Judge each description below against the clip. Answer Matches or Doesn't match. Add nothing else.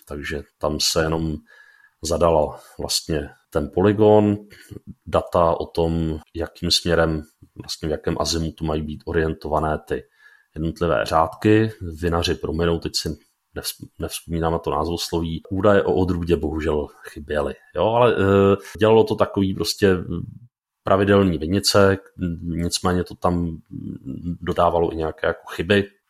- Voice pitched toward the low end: Matches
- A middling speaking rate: Matches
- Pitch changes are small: Doesn't match